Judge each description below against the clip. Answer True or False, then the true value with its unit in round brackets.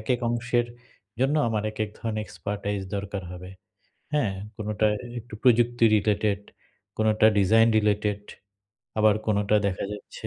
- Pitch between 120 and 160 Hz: False (105 Hz)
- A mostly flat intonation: True (1.9 semitones)